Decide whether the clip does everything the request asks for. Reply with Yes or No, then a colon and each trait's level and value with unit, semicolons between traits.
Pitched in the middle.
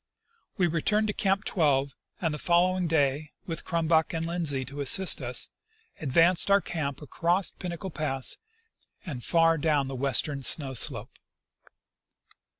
Yes: medium, 160 Hz